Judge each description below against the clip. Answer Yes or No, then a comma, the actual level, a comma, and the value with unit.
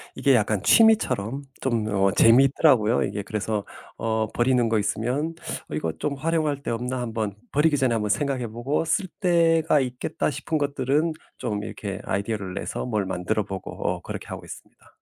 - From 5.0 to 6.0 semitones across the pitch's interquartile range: Yes, average, 5.3 semitones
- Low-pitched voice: Yes, low, 120 Hz